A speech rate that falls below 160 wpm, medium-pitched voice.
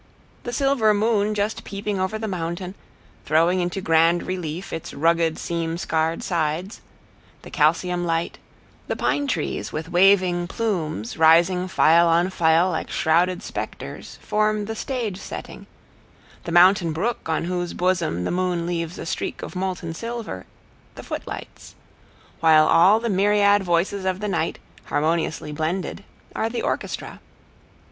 Yes: average, 140 wpm; medium, 180 Hz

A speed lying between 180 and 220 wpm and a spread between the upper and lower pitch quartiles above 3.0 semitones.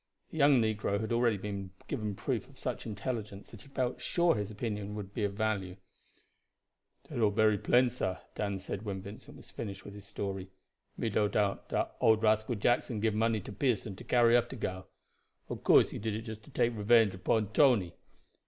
No: average, 190 wpm; narrow, 2.4 semitones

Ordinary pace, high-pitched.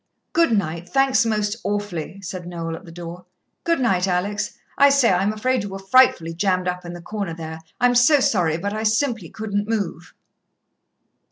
Yes: average, 180 wpm; high, 200 Hz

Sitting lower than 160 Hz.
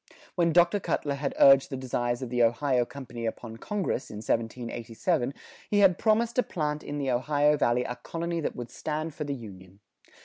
Yes: low, 135 Hz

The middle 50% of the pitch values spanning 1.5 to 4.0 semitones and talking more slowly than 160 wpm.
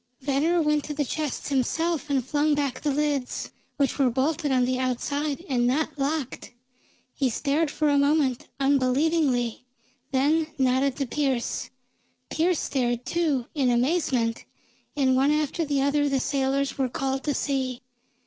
Yes: narrow, 2.5 semitones; average, 150 wpm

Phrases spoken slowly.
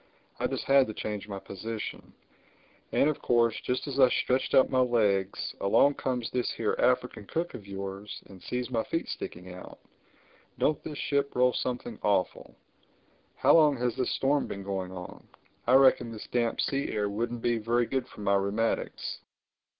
No: average, 175 wpm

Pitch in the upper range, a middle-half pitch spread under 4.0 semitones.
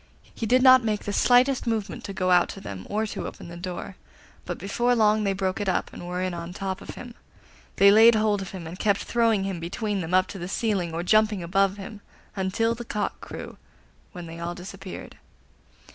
Yes: high, 195 Hz; average, 3.3 semitones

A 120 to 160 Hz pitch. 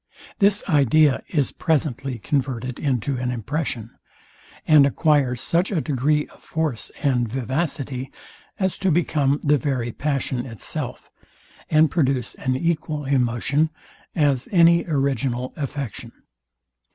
Yes: medium, 140 Hz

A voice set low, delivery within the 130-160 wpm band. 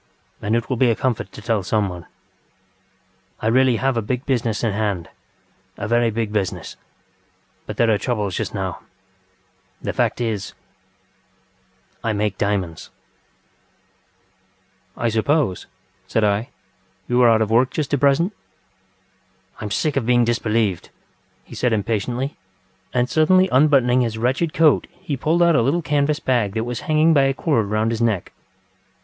Yes: low, 115 Hz; average, 155 wpm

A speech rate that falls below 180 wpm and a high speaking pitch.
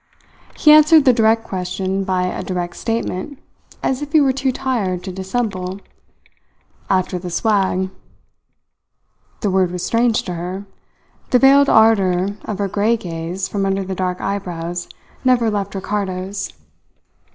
Yes: average, 140 wpm; high, 195 Hz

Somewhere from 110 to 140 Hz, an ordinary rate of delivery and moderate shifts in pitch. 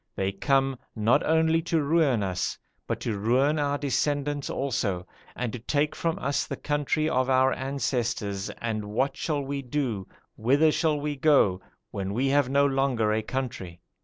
Yes: low, 135 Hz; average, 165 wpm; average, 4.5 semitones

